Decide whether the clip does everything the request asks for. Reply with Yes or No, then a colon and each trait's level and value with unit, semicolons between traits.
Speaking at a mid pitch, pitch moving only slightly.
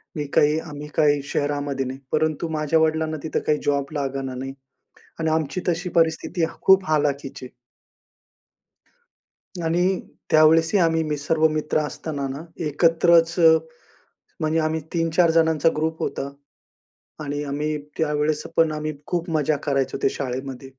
Yes: medium, 155 Hz; narrow, 2.0 semitones